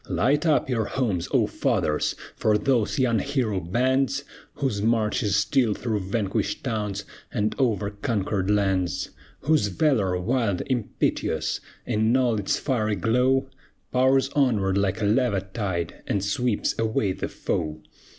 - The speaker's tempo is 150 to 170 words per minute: No, average, 140 wpm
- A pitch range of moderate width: Yes, average, 4.3 semitones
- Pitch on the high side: No, low, 110 Hz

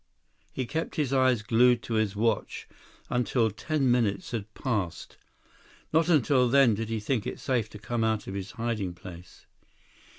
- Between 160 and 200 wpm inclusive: Yes, average, 165 wpm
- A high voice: No, low, 115 Hz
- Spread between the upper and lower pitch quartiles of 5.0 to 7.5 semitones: No, average, 3.5 semitones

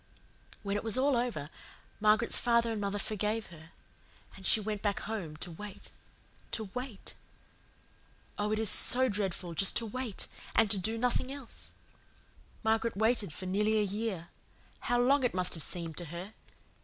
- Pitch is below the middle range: No, high, 210 Hz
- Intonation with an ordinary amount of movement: Yes, average, 3.3 semitones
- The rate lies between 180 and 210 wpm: No, average, 165 wpm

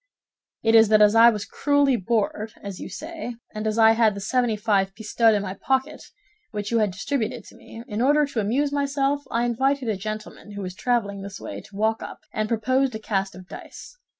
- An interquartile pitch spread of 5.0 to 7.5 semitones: No, average, 3.8 semitones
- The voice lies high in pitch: Yes, high, 225 Hz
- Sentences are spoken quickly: Yes, fast, 215 wpm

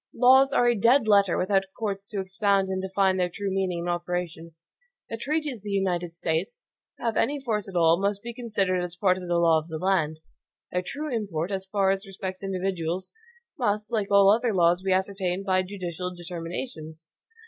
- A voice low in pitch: No, high, 190 Hz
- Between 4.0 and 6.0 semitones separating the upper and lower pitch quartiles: No, average, 2.7 semitones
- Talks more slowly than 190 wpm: No, average, 195 wpm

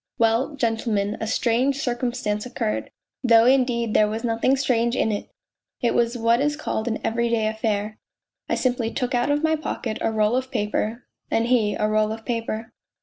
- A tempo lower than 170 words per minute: No, average, 185 wpm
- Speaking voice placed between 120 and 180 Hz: No, high, 230 Hz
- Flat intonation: Yes, narrow, 2.3 semitones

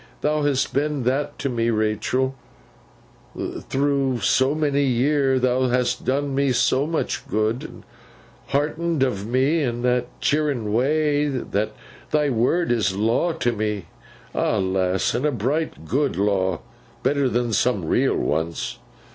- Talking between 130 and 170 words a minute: Yes, average, 145 wpm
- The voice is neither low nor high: No, low, 130 Hz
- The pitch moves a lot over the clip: No, average, 4.6 semitones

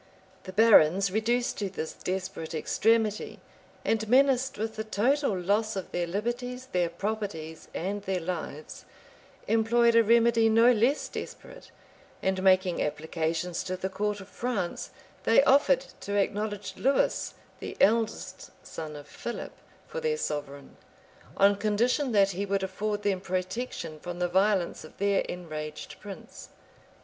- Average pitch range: Yes, average, 4.0 semitones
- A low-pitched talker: No, high, 200 Hz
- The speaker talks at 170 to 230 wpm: No, average, 140 wpm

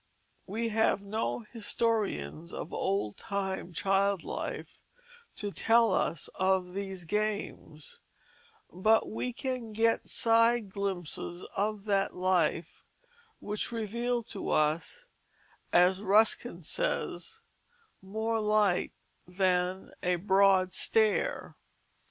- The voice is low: No, high, 200 Hz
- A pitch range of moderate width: Yes, average, 3.2 semitones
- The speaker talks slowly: Yes, slow, 100 wpm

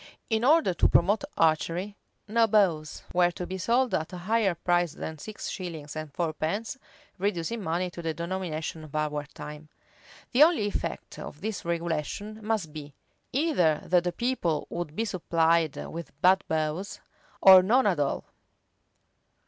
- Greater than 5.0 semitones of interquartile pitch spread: No, average, 4.7 semitones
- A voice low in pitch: No, medium, 175 Hz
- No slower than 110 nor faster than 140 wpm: No, average, 155 wpm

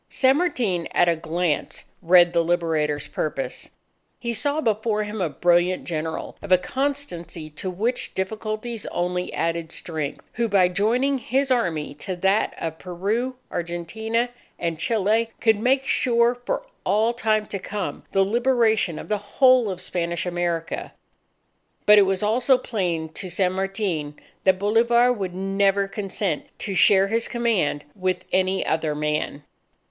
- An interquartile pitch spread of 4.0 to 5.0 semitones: Yes, average, 4.7 semitones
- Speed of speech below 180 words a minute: Yes, average, 150 wpm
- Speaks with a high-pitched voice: Yes, high, 195 Hz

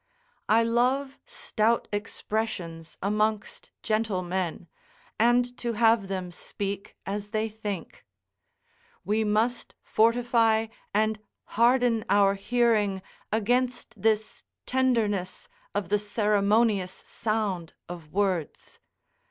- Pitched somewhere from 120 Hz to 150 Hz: No, high, 215 Hz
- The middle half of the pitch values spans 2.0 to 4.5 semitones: Yes, average, 2.7 semitones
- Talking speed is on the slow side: Yes, slow, 95 wpm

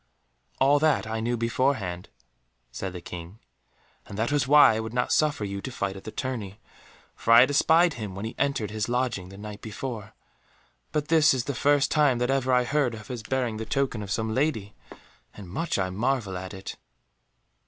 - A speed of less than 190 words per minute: No, average, 200 wpm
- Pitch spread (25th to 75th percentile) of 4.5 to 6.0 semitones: Yes, average, 4.9 semitones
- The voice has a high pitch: No, low, 115 Hz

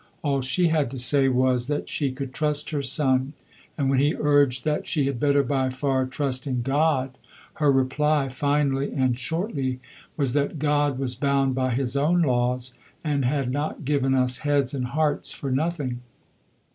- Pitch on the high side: No, low, 135 Hz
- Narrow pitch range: Yes, narrow, 2.2 semitones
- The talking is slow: No, average, 175 wpm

